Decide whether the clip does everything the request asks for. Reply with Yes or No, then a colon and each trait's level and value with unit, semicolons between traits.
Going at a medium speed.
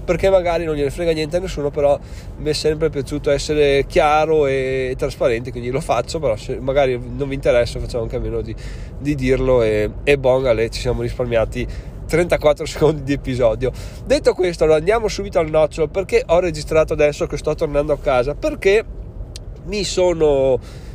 No: fast, 180 wpm